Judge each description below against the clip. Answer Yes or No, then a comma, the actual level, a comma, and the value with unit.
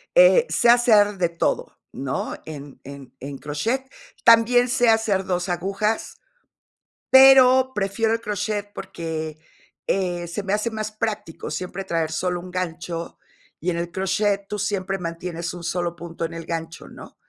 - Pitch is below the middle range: No, medium, 185 Hz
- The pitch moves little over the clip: No, average, 4.3 semitones